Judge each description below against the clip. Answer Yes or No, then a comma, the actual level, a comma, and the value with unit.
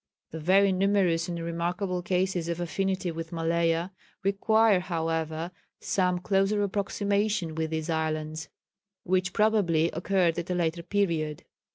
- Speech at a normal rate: No, slow, 130 wpm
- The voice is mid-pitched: Yes, medium, 175 Hz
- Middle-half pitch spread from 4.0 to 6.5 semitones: No, average, 2.9 semitones